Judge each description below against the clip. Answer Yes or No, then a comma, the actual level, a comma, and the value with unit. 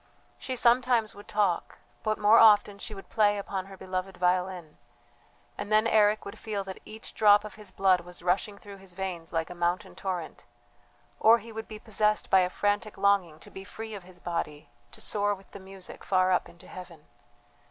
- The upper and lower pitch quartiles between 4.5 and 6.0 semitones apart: No, average, 2.7 semitones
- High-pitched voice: Yes, high, 195 Hz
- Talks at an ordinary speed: Yes, average, 195 wpm